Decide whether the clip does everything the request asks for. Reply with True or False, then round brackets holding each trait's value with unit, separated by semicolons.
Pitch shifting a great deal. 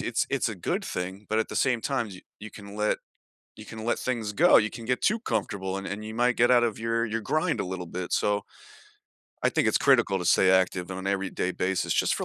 False (3.4 semitones)